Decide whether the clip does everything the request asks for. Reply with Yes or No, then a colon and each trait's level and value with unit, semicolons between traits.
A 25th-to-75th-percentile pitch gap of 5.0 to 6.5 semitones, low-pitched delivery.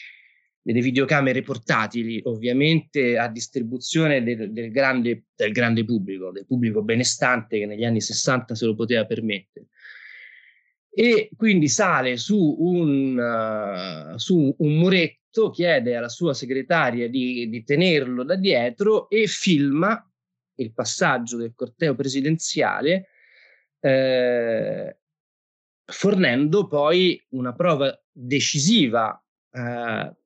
Yes: wide, 5.4 semitones; low, 130 Hz